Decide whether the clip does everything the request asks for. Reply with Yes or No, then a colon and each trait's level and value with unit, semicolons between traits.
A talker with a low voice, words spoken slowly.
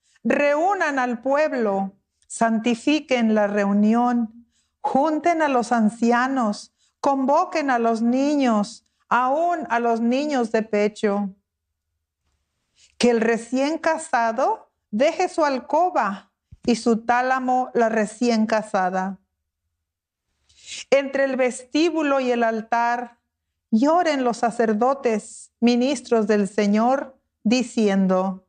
No: high, 235 Hz; slow, 95 wpm